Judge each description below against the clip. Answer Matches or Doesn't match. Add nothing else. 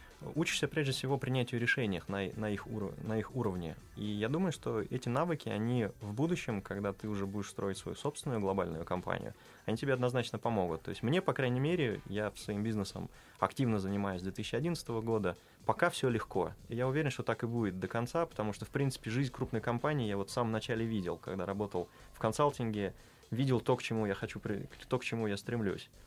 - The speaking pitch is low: Matches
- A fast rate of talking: Matches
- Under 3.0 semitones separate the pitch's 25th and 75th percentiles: Doesn't match